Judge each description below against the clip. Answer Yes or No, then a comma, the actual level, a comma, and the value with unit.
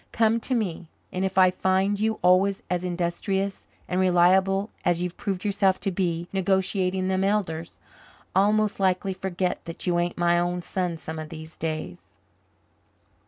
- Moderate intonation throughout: No, narrow, 2.0 semitones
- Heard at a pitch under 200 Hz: Yes, medium, 185 Hz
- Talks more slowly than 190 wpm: Yes, average, 165 wpm